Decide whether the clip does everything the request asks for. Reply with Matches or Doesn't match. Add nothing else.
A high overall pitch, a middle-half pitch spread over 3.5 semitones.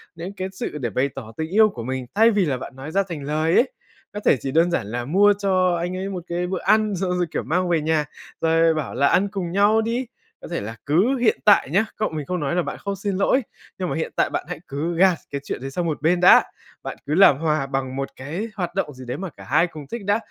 Doesn't match